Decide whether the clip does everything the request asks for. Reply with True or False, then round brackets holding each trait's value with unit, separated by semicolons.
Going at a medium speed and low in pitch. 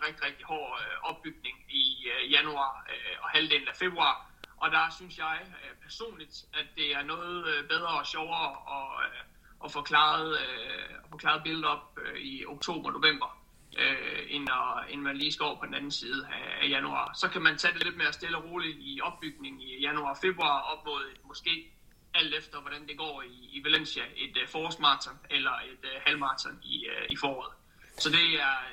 False (165 wpm; 160 Hz)